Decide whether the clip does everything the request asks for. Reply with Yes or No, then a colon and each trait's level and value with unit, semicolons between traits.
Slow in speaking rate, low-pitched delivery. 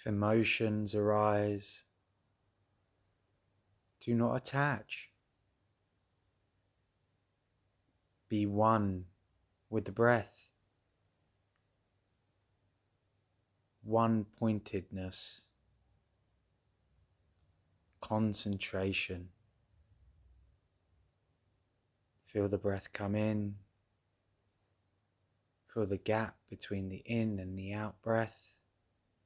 Yes: slow, 60 wpm; low, 100 Hz